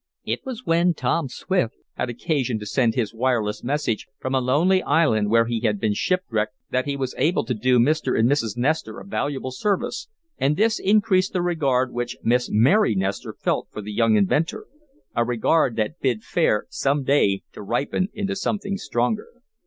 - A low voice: Yes, low, 130 Hz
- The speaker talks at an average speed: Yes, average, 185 wpm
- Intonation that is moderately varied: No, wide, 6.7 semitones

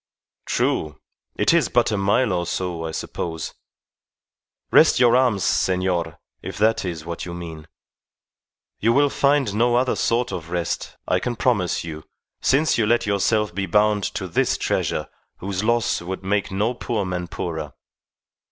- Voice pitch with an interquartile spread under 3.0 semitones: No, average, 5.0 semitones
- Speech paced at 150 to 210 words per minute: Yes, average, 160 wpm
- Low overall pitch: Yes, low, 100 Hz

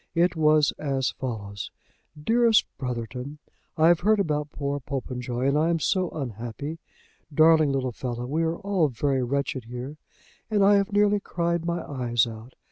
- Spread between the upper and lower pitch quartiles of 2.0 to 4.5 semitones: No, average, 5.1 semitones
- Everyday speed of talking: Yes, average, 160 wpm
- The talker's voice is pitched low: No, medium, 145 Hz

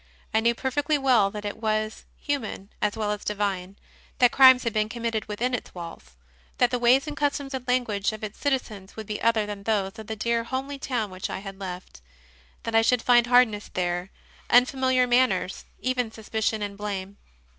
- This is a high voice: Yes, high, 220 Hz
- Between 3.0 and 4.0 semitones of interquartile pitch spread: Yes, average, 3.4 semitones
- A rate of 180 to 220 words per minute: Yes, average, 190 wpm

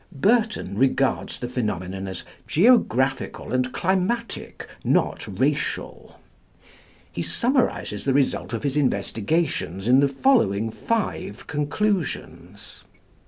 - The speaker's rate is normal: No, slow, 100 wpm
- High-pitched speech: No, low, 135 Hz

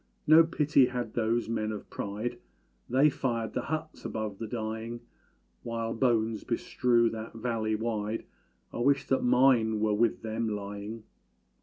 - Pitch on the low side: Yes, low, 115 Hz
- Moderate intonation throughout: No, narrow, 2.1 semitones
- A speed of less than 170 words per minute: Yes, average, 145 wpm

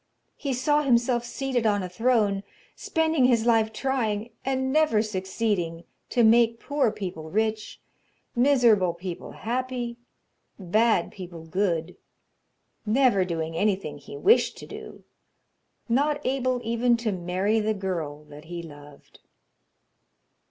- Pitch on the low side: No, high, 220 Hz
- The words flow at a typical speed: No, slow, 125 wpm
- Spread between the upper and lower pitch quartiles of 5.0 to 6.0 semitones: Yes, average, 5.3 semitones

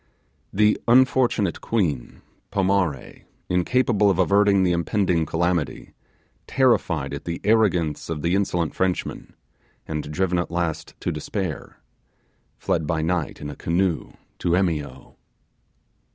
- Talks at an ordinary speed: No, slow, 120 wpm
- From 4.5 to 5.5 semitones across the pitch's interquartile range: No, average, 3.5 semitones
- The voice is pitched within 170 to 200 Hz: No, very low, 90 Hz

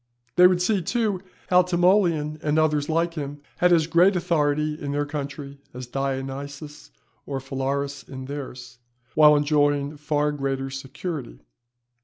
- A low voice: No, medium, 145 Hz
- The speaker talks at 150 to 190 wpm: No, average, 140 wpm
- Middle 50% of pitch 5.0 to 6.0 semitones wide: No, average, 3.2 semitones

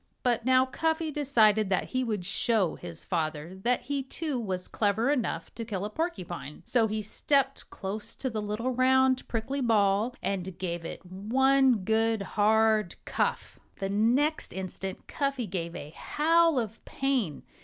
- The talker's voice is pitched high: Yes, high, 220 Hz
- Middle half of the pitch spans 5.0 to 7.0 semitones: Yes, average, 5.3 semitones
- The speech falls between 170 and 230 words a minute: No, average, 155 wpm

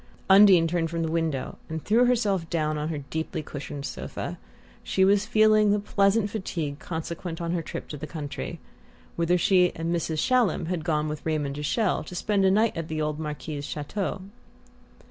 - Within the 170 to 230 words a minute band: Yes, average, 185 wpm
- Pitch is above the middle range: No, medium, 165 Hz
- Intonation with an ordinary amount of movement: Yes, average, 4.2 semitones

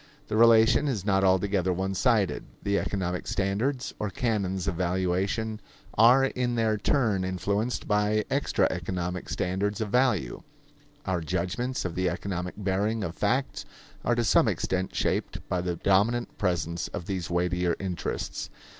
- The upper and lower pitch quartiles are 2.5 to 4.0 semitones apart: Yes, average, 3.5 semitones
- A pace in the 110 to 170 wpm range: Yes, average, 145 wpm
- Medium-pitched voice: No, low, 100 Hz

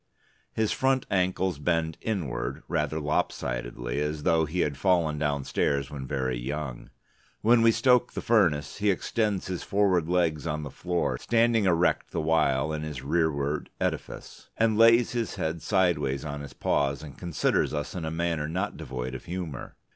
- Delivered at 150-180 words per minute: Yes, average, 165 wpm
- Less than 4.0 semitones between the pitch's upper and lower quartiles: No, average, 4.5 semitones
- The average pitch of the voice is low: Yes, very low, 80 Hz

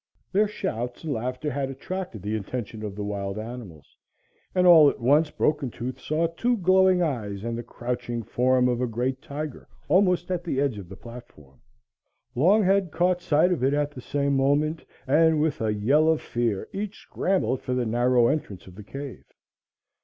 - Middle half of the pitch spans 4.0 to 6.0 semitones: Yes, wide, 5.6 semitones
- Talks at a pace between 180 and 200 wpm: Yes, average, 185 wpm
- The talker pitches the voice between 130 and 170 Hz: Yes, low, 135 Hz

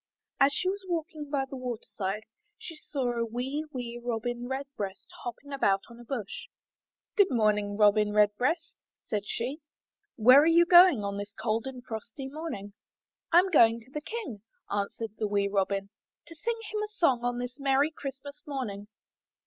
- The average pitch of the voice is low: No, high, 245 Hz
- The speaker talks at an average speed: Yes, average, 170 wpm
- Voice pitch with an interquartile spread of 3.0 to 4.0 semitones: No, wide, 5.5 semitones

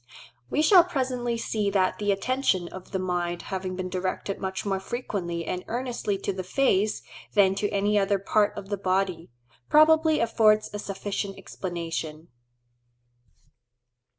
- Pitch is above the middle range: Yes, high, 200 Hz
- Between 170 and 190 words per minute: No, average, 145 wpm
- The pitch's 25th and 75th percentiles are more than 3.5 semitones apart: No, average, 3.1 semitones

